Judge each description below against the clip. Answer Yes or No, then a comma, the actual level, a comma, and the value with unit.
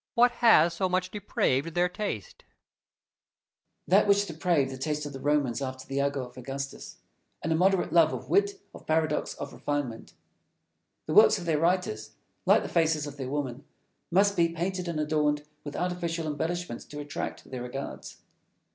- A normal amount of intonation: Yes, average, 4.3 semitones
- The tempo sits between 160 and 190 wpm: Yes, average, 170 wpm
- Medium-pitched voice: Yes, medium, 155 Hz